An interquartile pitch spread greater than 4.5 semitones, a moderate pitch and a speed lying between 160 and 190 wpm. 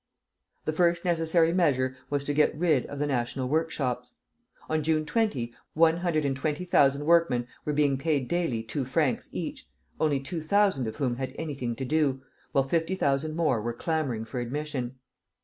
No: average, 3.7 semitones; medium, 145 Hz; average, 175 wpm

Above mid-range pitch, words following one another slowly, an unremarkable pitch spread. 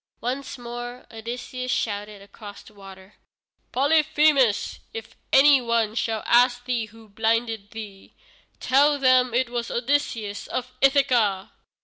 Yes: high, 240 Hz; slow, 120 wpm; average, 3.0 semitones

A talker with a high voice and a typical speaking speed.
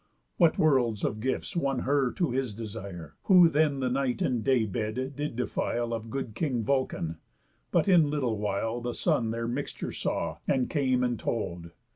No: low, 125 Hz; average, 175 wpm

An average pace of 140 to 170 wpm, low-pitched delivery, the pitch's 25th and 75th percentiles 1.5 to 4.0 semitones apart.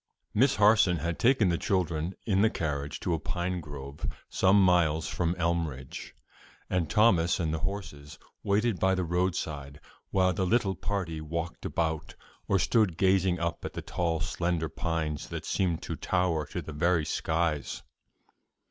Yes: average, 155 wpm; very low, 85 Hz; average, 3.0 semitones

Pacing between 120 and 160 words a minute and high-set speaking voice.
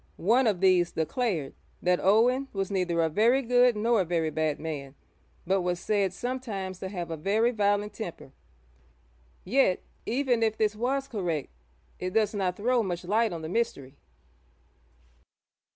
Yes: average, 155 wpm; high, 195 Hz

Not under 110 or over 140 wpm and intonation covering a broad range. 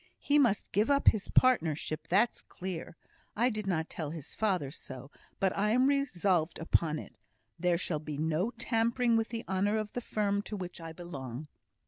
No: average, 180 wpm; wide, 5.8 semitones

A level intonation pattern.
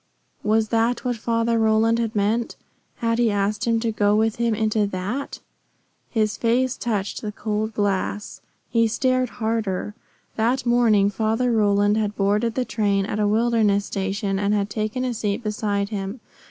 Yes: narrow, 2.1 semitones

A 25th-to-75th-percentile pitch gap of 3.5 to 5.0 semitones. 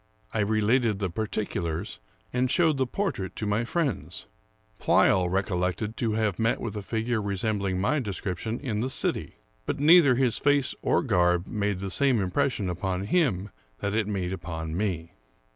Yes: average, 4.5 semitones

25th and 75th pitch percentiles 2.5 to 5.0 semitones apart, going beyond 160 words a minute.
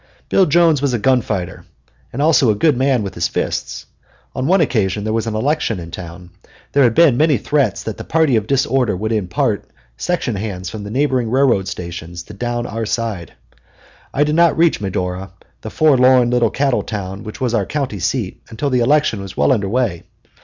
No: wide, 5.6 semitones; average, 200 wpm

